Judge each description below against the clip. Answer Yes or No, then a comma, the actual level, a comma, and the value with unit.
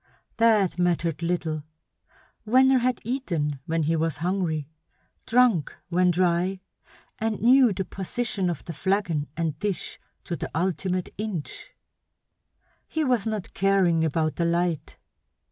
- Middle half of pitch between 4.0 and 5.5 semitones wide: Yes, average, 4.5 semitones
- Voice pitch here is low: No, medium, 180 Hz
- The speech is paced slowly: Yes, slow, 130 wpm